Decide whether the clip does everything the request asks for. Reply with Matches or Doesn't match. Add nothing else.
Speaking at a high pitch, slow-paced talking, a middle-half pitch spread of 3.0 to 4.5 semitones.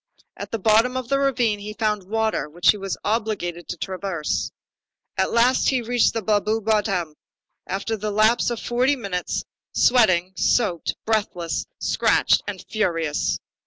Doesn't match